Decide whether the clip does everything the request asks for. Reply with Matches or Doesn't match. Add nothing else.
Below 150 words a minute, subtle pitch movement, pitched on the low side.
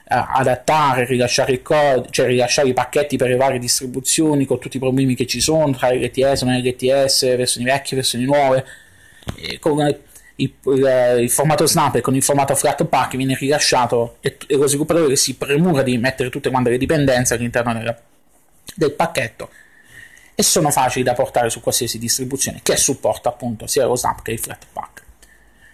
Doesn't match